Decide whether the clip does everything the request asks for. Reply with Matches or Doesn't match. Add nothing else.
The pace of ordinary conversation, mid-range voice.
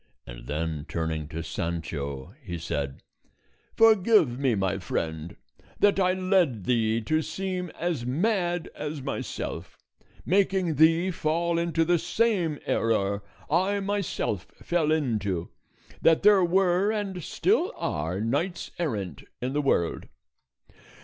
Doesn't match